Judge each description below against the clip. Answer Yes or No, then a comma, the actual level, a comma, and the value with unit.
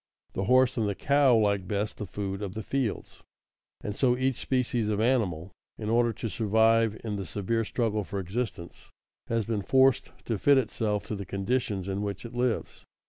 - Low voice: Yes, low, 110 Hz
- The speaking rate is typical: Yes, average, 190 wpm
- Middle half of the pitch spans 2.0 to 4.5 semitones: Yes, average, 3.3 semitones